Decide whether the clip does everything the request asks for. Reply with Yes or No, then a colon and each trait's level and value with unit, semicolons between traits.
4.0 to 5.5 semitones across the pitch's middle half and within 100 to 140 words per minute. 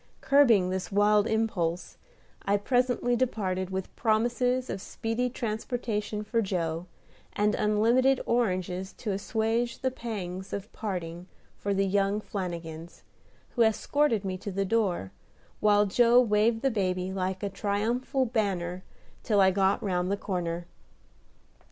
No: average, 3.5 semitones; slow, 135 wpm